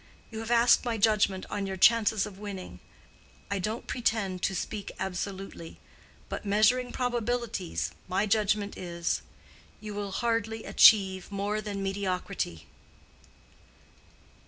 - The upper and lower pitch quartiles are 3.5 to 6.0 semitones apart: No, narrow, 2.6 semitones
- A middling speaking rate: No, slow, 115 wpm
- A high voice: Yes, high, 205 Hz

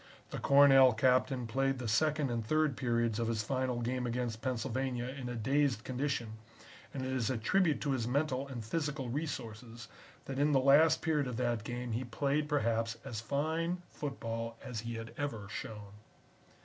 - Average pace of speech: Yes, average, 175 wpm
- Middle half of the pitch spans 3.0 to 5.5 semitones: Yes, average, 3.4 semitones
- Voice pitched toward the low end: Yes, low, 125 Hz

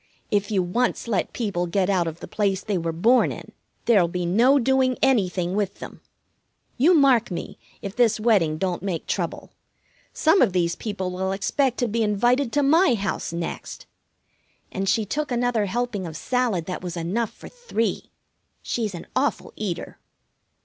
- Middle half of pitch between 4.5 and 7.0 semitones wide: Yes, average, 5.2 semitones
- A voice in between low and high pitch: No, high, 205 Hz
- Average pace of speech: Yes, average, 170 wpm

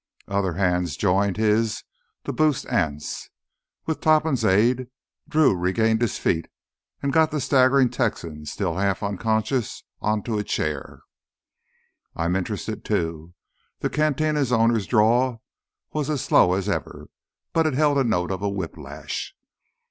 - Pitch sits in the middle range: No, low, 110 Hz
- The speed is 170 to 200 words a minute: No, slow, 135 wpm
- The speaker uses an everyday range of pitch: No, wide, 6.0 semitones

